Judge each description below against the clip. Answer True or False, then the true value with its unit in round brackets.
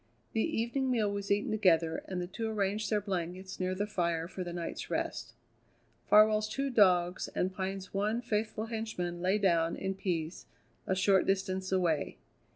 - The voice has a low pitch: False (195 Hz)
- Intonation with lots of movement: False (3.0 semitones)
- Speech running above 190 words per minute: False (165 wpm)